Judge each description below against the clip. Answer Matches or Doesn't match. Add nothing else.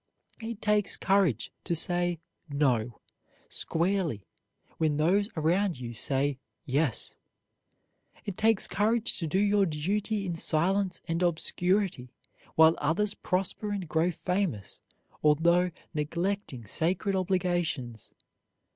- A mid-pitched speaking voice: Matches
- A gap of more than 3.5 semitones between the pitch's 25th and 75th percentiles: Matches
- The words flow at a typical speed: Doesn't match